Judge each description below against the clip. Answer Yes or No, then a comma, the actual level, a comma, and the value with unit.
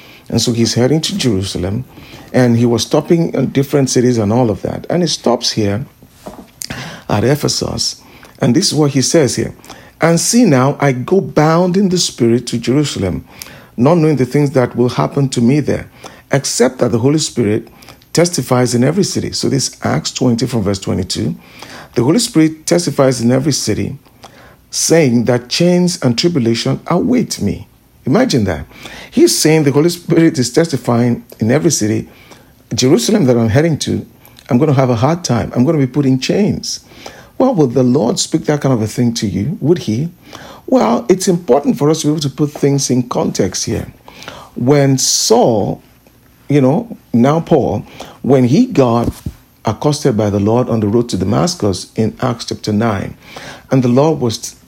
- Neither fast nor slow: Yes, average, 185 wpm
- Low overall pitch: Yes, low, 130 Hz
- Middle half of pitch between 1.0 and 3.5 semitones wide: No, average, 4.8 semitones